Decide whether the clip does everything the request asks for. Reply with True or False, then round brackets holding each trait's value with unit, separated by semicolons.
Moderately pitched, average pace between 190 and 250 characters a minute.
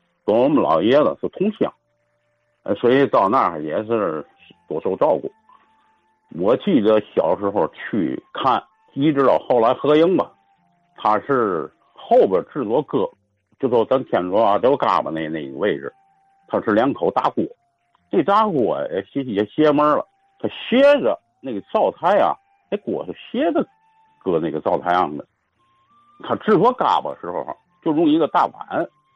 True (155 Hz; 220 characters per minute)